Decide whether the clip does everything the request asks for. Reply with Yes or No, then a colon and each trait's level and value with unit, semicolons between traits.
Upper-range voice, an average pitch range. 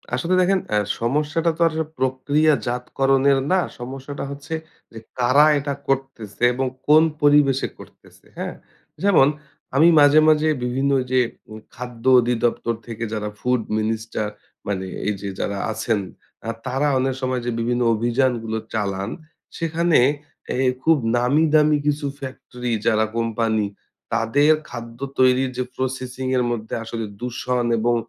No: low, 125 Hz; average, 3.7 semitones